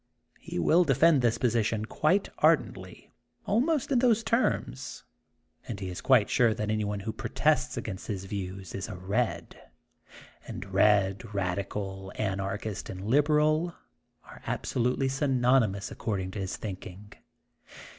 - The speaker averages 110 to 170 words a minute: Yes, average, 140 wpm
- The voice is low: Yes, low, 105 Hz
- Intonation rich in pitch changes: Yes, wide, 5.7 semitones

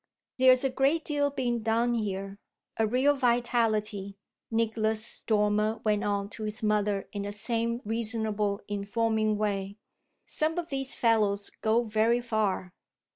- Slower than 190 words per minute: Yes, slow, 135 wpm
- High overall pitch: Yes, high, 220 Hz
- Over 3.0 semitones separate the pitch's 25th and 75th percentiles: No, narrow, 2.5 semitones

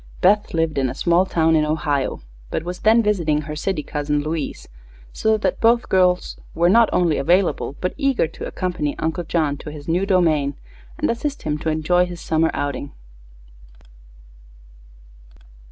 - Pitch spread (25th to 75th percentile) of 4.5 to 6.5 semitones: No, average, 3.5 semitones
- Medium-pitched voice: Yes, medium, 165 Hz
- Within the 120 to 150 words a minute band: No, average, 160 wpm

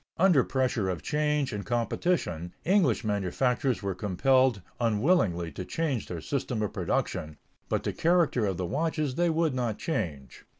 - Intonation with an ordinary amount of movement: No, wide, 7.6 semitones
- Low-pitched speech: Yes, low, 120 Hz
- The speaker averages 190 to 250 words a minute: No, average, 155 wpm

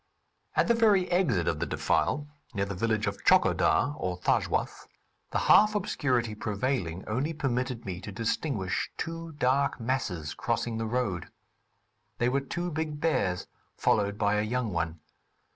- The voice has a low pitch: Yes, low, 120 Hz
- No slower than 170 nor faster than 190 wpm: No, average, 150 wpm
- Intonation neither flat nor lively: No, wide, 6.6 semitones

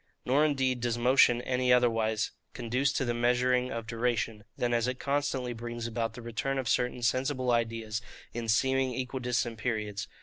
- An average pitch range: No, narrow, 1.8 semitones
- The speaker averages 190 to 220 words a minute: No, average, 165 wpm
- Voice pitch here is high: No, low, 120 Hz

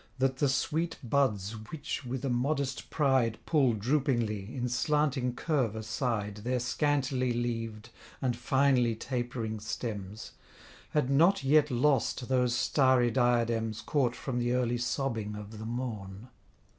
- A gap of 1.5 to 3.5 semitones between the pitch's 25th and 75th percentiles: Yes, average, 3.0 semitones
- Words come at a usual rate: No, slow, 130 wpm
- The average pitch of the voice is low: Yes, low, 125 Hz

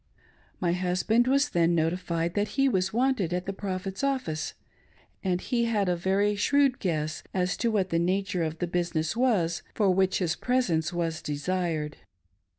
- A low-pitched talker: No, medium, 185 Hz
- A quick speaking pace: No, average, 160 wpm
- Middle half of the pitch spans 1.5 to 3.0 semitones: No, average, 3.7 semitones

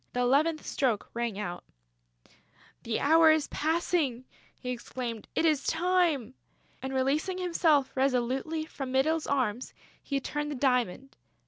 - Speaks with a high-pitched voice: Yes, very high, 275 Hz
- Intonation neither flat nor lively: Yes, average, 4.0 semitones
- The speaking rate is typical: No, slow, 130 wpm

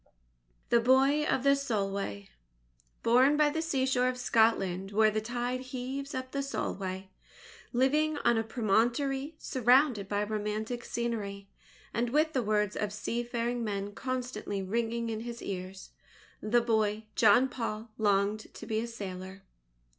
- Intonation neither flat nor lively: Yes, average, 3.7 semitones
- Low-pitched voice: No, high, 230 Hz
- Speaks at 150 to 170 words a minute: No, average, 140 wpm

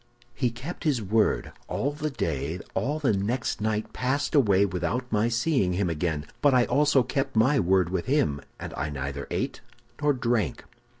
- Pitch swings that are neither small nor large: No, wide, 6.8 semitones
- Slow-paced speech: No, average, 175 wpm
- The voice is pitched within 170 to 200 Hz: No, low, 115 Hz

